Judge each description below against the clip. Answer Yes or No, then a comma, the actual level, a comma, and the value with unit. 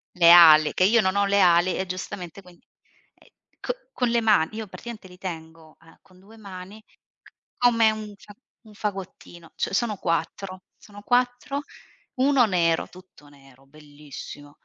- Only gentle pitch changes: No, average, 4.5 semitones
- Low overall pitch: No, medium, 185 Hz